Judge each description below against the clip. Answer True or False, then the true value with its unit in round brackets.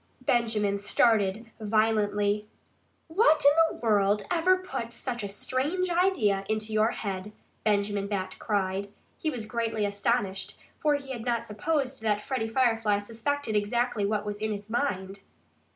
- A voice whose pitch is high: True (220 Hz)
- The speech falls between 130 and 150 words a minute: True (145 wpm)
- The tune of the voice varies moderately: True (3.7 semitones)